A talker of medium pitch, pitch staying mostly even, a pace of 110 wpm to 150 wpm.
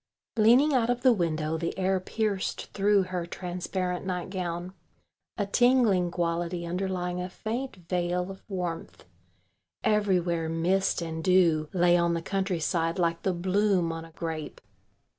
Yes: medium, 180 Hz; narrow, 2.3 semitones; average, 140 wpm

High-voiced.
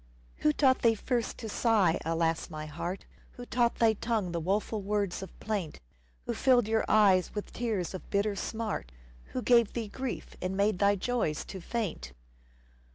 Yes: high, 205 Hz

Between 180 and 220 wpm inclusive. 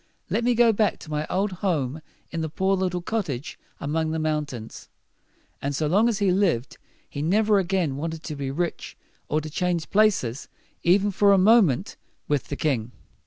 Yes: average, 185 wpm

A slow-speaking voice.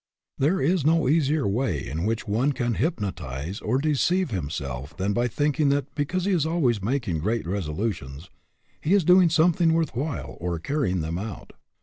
No: average, 180 wpm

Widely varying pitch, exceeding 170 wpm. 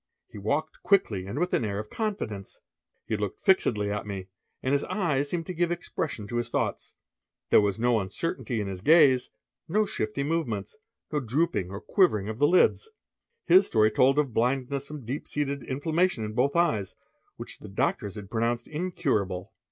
Yes: wide, 7.1 semitones; average, 180 wpm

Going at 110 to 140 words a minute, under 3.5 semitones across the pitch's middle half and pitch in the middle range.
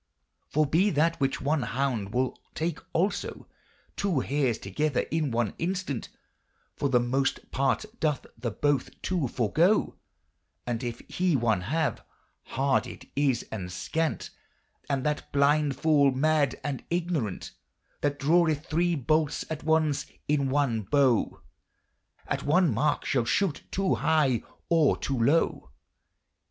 No: slow, 135 wpm; average, 3.8 semitones; medium, 145 Hz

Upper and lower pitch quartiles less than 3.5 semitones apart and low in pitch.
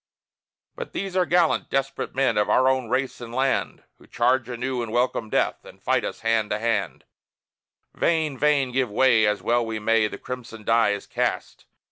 Yes: average, 2.9 semitones; low, 120 Hz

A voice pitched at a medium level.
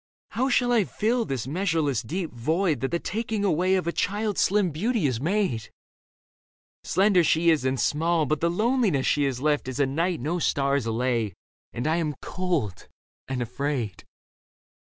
Yes: medium, 160 Hz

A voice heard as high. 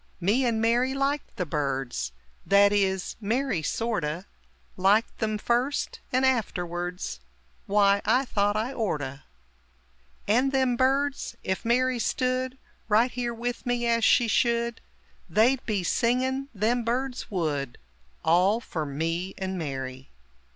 Yes: high, 220 Hz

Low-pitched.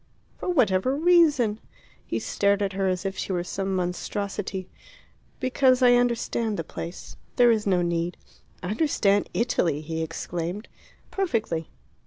No: high, 200 Hz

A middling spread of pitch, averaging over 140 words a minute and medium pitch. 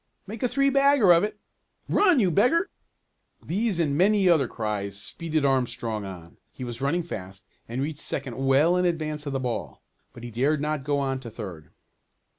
No: wide, 7.0 semitones; average, 185 wpm; medium, 145 Hz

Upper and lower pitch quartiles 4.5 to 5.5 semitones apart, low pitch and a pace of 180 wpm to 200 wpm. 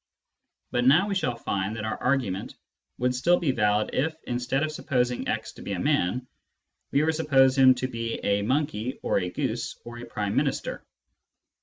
No: average, 4.1 semitones; low, 125 Hz; average, 195 wpm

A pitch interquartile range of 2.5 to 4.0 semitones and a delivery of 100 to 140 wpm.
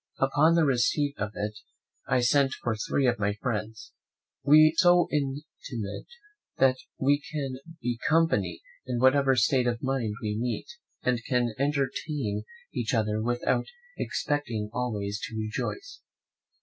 No: average, 4.4 semitones; slow, 135 wpm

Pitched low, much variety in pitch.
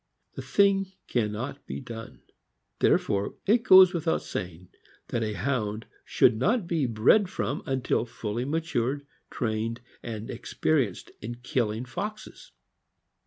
Yes: low, 125 Hz; wide, 7.0 semitones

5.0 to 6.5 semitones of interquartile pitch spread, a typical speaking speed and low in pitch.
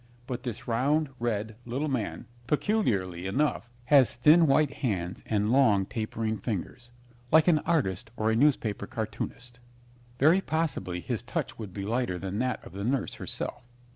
Yes: average, 5.3 semitones; average, 155 wpm; low, 120 Hz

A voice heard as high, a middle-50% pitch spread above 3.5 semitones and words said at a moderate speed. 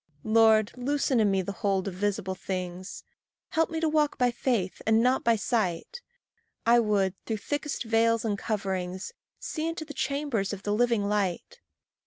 Yes: high, 220 Hz; average, 4.8 semitones; average, 170 wpm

